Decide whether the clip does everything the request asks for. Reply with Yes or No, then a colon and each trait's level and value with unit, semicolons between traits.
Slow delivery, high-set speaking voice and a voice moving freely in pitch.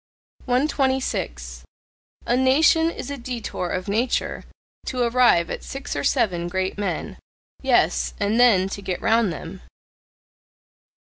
Yes: slow, 125 wpm; high, 215 Hz; wide, 6.2 semitones